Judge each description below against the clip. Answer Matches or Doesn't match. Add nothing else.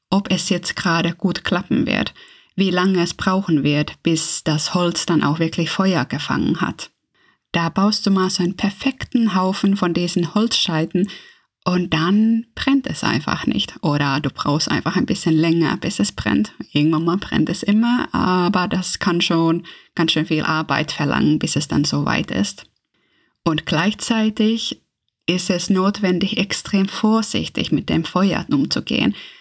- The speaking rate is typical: Matches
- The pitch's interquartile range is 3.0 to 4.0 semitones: Matches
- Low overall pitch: Doesn't match